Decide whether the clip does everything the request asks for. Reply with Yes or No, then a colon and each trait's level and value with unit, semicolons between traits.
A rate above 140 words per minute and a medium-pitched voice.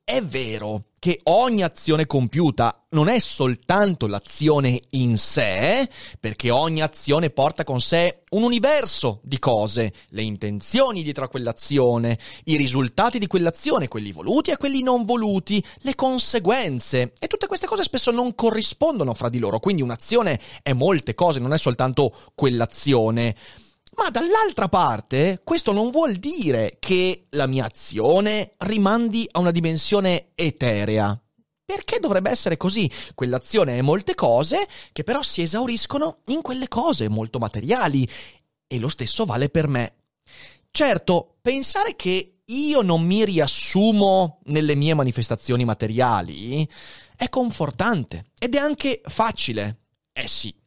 No: average, 135 wpm; medium, 160 Hz